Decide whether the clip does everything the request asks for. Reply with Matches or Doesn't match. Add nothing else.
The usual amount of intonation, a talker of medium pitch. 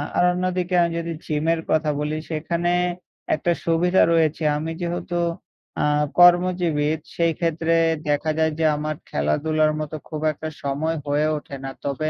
Doesn't match